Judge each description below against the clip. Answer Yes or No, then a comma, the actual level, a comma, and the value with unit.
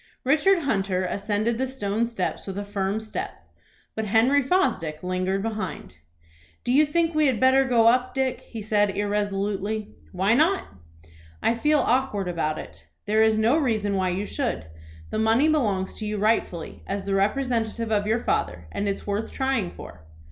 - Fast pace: No, average, 175 wpm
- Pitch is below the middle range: No, high, 215 Hz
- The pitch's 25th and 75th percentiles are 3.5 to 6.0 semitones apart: Yes, average, 4.3 semitones